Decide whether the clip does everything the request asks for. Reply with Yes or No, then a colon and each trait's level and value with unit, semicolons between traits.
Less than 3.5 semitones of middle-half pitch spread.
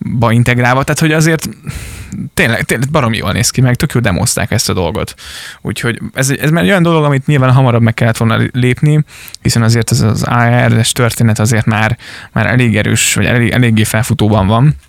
Yes: average, 2.8 semitones